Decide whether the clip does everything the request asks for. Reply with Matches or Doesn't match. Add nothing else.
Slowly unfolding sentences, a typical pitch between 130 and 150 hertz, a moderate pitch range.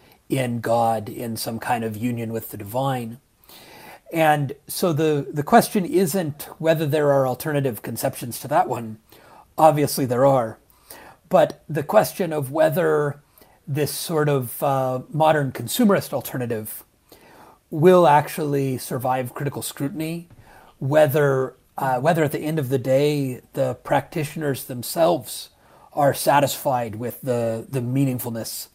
Matches